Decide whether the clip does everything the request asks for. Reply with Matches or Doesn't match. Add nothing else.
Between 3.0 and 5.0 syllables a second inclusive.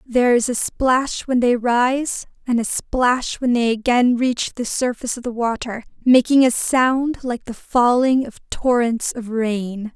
Matches